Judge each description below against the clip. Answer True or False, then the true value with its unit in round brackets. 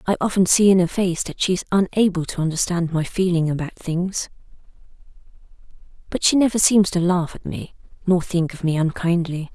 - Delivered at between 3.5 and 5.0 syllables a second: False (5.4 syllables/s)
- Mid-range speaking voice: True (175 Hz)